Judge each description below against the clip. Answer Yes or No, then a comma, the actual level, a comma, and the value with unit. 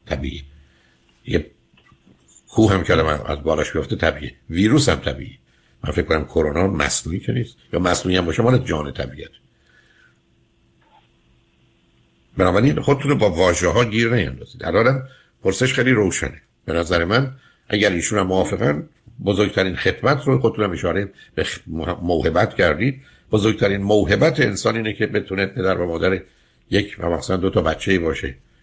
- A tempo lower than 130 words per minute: No, average, 150 wpm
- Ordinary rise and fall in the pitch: No, wide, 5.8 semitones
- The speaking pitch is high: No, very low, 95 Hz